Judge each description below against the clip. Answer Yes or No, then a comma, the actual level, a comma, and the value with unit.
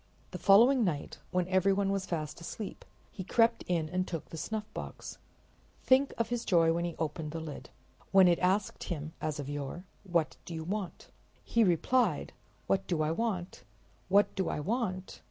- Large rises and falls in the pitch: No, average, 3.8 semitones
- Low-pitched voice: No, medium, 180 Hz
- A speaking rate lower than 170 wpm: No, average, 175 wpm